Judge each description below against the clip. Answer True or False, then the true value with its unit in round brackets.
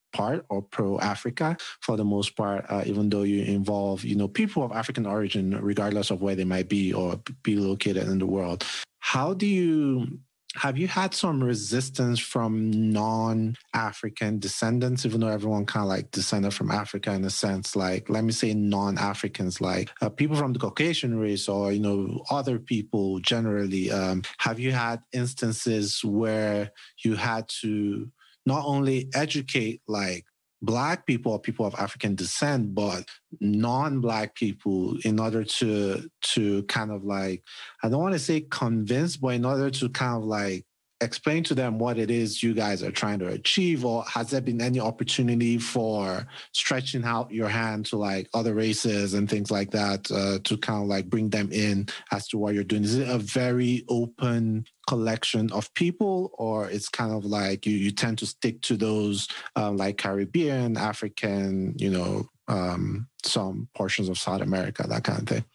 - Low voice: True (110 Hz)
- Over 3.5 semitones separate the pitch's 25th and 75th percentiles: False (3.2 semitones)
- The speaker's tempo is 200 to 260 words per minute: False (180 wpm)